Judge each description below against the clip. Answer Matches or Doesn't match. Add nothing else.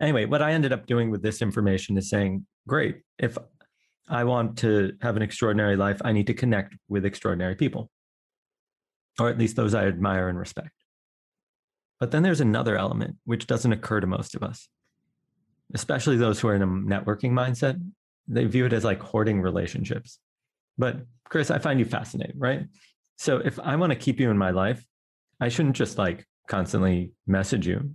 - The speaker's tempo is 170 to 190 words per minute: Matches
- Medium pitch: Doesn't match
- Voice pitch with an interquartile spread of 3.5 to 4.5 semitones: Matches